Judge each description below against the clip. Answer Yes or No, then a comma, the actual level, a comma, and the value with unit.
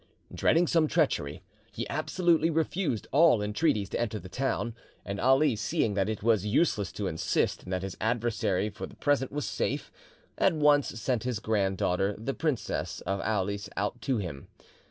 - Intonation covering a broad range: Yes, wide, 6.3 semitones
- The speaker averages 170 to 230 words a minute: Yes, average, 175 wpm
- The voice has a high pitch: No, low, 110 Hz